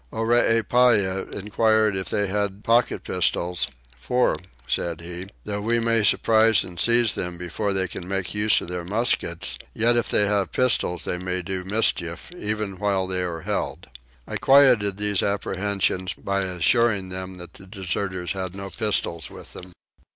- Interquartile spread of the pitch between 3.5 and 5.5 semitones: No, average, 3.0 semitones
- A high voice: No, low, 100 Hz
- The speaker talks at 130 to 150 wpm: No, average, 160 wpm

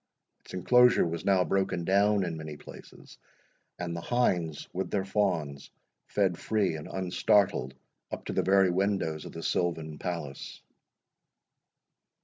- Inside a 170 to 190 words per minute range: No, slow, 135 wpm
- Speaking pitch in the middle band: No, very low, 90 Hz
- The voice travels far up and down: No, average, 3.3 semitones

